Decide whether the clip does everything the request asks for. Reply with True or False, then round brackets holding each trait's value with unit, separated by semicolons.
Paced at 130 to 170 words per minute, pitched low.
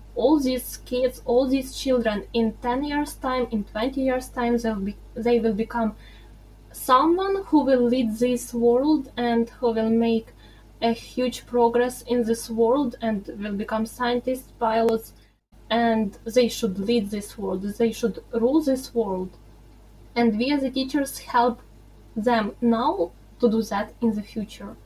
False (155 wpm; 235 Hz)